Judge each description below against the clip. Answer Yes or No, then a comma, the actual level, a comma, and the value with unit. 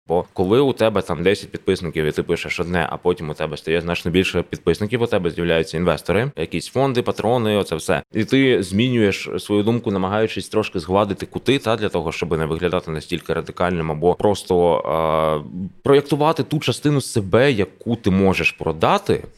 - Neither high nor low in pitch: No, very low, 95 Hz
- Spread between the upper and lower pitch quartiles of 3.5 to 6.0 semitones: Yes, average, 4.6 semitones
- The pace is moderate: No, fast, 175 wpm